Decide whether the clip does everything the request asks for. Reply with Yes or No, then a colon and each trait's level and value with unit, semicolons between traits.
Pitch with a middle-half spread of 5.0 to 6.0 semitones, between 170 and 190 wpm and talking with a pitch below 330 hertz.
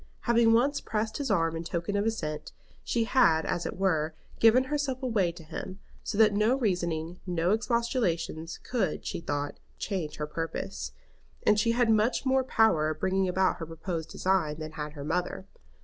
Yes: wide, 5.6 semitones; average, 180 wpm; medium, 185 Hz